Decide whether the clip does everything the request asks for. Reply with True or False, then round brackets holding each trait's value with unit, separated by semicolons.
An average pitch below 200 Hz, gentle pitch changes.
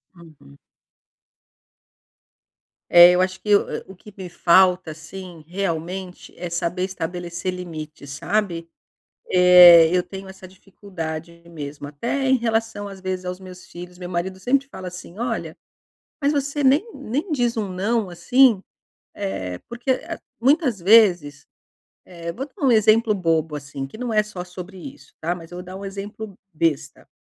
False (185 Hz; 4.1 semitones)